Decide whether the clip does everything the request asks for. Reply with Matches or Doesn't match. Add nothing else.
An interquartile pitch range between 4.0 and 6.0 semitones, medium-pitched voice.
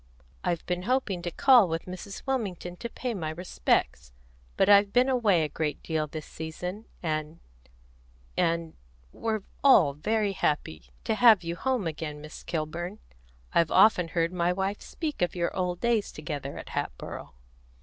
Matches